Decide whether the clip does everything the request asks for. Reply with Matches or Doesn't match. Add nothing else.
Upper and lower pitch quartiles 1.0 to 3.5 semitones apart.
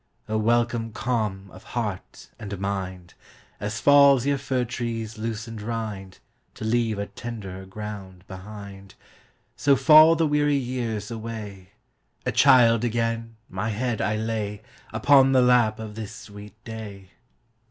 Matches